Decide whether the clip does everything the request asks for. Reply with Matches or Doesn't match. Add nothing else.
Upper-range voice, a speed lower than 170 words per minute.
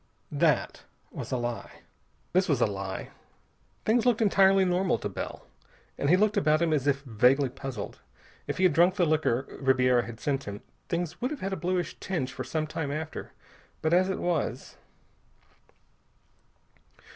Doesn't match